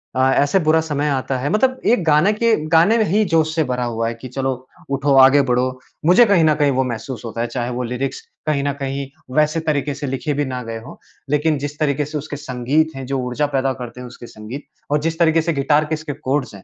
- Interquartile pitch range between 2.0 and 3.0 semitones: No, average, 3.4 semitones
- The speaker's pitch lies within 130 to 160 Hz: Yes, medium, 140 Hz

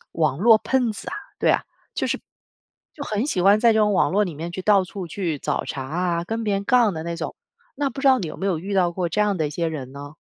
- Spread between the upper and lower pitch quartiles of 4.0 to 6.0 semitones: Yes, average, 4.3 semitones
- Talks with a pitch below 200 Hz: Yes, high, 190 Hz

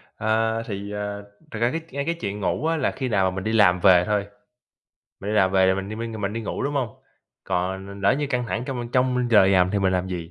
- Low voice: Yes, low, 105 Hz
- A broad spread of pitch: No, average, 3.8 semitones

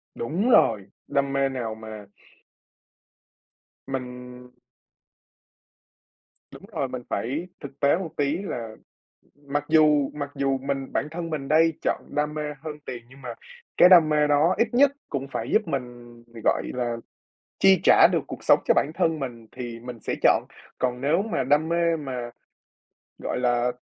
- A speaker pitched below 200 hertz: Yes, medium, 140 Hz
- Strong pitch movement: No, average, 3.9 semitones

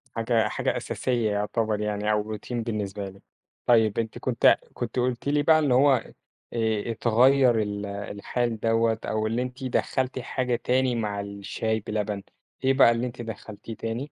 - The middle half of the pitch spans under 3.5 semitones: Yes, average, 2.8 semitones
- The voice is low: Yes, low, 115 Hz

